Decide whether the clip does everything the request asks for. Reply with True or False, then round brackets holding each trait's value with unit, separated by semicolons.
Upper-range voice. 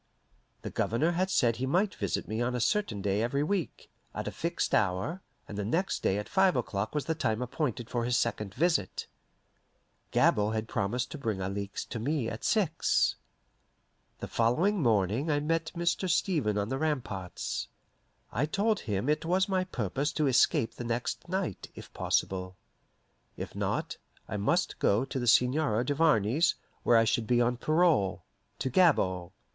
False (125 Hz)